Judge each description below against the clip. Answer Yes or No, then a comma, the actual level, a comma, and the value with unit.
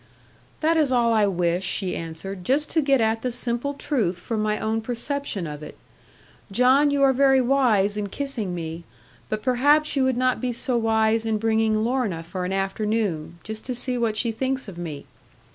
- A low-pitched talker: No, high, 225 Hz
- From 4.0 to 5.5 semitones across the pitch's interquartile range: Yes, average, 4.9 semitones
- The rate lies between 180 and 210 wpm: Yes, average, 195 wpm